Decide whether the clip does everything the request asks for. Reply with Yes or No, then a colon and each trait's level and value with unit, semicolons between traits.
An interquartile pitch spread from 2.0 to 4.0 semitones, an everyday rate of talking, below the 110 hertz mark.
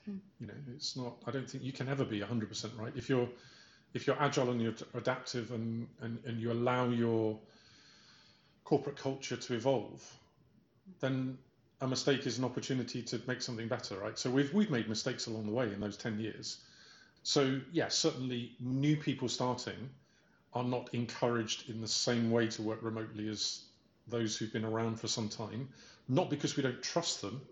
No: average, 2.7 semitones; average, 190 wpm; low, 125 Hz